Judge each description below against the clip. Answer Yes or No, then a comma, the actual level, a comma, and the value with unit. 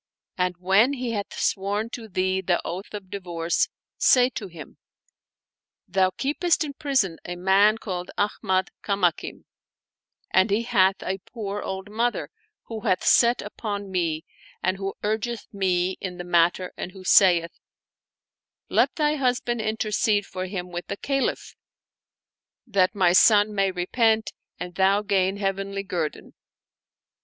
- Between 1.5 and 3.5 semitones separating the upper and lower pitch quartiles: Yes, average, 2.9 semitones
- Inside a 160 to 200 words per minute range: No, average, 140 wpm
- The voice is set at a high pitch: Yes, high, 195 Hz